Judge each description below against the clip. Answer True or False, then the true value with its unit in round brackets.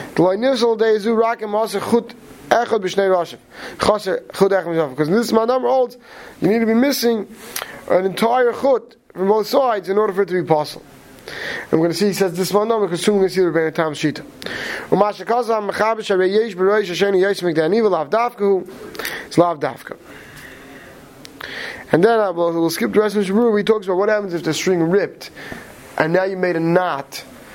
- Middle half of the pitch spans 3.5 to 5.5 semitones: True (4.0 semitones)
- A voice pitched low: False (205 Hz)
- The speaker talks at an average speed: True (155 wpm)